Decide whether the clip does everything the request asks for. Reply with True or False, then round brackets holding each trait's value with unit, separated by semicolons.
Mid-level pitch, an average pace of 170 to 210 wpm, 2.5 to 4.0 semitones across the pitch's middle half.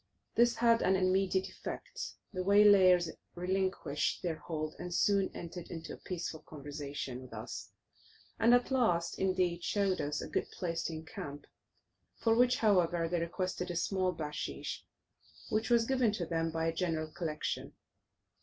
False (180 Hz; 155 wpm; 3.4 semitones)